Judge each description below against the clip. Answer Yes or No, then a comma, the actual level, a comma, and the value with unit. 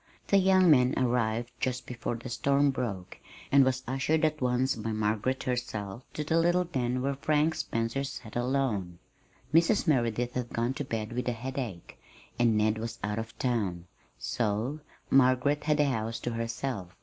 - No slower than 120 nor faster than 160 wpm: No, average, 170 wpm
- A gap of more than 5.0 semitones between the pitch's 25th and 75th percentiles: No, average, 3.5 semitones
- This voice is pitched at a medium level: No, low, 125 Hz